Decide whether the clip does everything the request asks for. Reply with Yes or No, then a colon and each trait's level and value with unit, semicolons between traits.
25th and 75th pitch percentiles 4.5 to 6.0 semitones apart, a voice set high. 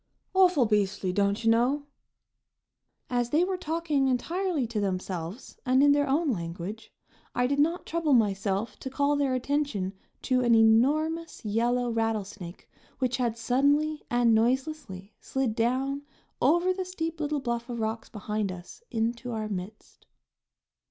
Yes: average, 4.9 semitones; high, 245 Hz